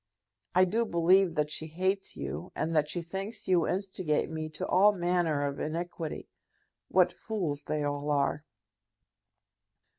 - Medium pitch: Yes, medium, 170 Hz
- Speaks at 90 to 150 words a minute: Yes, average, 145 wpm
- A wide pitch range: No, average, 3.5 semitones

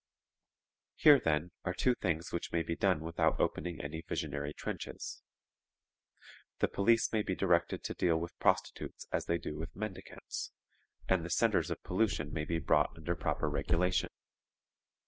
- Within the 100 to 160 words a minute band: Yes, average, 155 wpm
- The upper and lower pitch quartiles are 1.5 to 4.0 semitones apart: Yes, narrow, 2.6 semitones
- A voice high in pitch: No, very low, 85 Hz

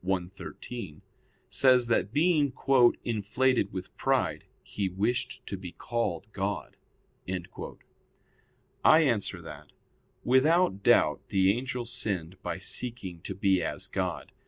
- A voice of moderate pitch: No, low, 100 Hz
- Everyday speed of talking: No, slow, 110 wpm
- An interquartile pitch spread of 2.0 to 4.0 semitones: No, average, 4.9 semitones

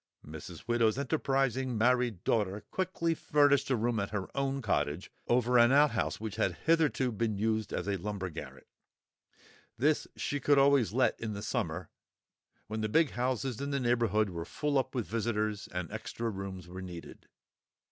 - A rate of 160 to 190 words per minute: Yes, average, 165 wpm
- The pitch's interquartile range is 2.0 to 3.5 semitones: No, average, 4.9 semitones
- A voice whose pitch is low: Yes, low, 115 Hz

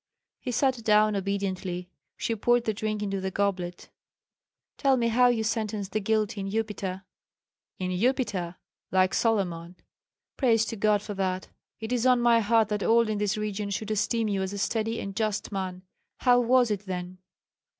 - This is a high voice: Yes, high, 210 Hz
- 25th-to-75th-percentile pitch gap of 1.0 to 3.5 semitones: Yes, average, 2.9 semitones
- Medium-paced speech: Yes, average, 175 wpm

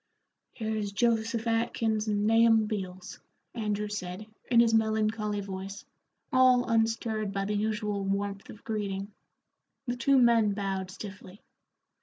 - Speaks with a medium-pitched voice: No, high, 215 Hz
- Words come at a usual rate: No, slow, 125 wpm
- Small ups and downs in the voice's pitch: Yes, narrow, 2.2 semitones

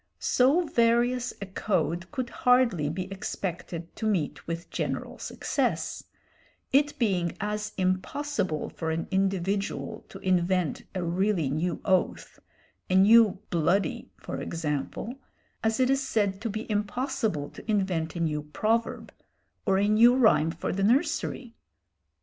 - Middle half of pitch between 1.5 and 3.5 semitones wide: No, average, 5.0 semitones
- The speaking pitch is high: Yes, high, 195 Hz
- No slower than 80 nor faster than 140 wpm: Yes, slow, 135 wpm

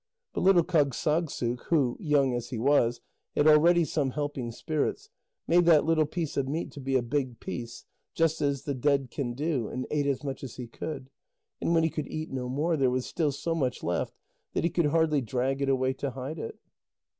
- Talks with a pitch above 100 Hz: Yes, medium, 140 Hz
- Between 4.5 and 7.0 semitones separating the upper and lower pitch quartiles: No, average, 3.6 semitones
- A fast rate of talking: Yes, fast, 210 wpm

